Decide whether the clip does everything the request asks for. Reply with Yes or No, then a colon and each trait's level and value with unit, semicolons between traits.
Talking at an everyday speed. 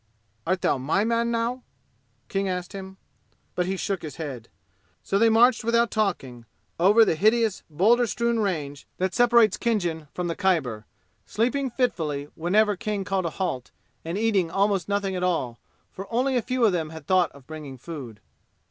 Yes: average, 175 wpm